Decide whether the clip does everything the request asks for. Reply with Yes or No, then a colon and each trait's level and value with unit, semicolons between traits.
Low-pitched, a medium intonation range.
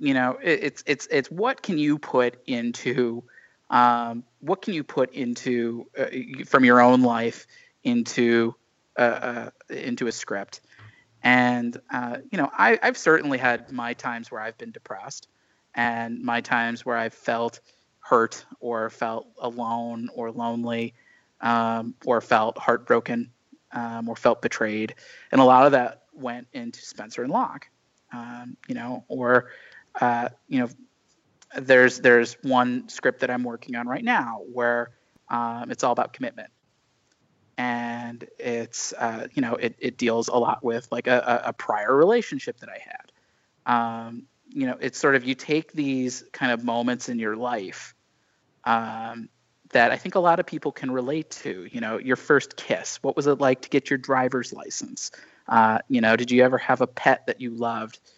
No: low, 120 Hz; narrow, 2.0 semitones